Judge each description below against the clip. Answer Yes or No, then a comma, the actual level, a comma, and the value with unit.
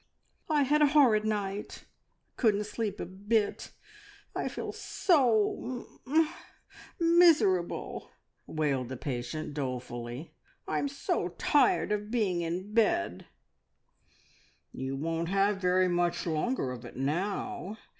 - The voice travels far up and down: Yes, wide, 7.2 semitones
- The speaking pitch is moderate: No, high, 195 Hz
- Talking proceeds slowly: Yes, slow, 120 wpm